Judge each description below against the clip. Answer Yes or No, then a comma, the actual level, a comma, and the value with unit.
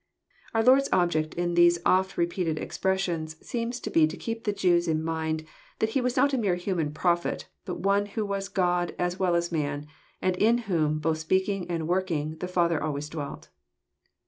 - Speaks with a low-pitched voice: No, medium, 175 Hz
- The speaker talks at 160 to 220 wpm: Yes, average, 195 wpm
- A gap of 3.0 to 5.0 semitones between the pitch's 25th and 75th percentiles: Yes, average, 3.6 semitones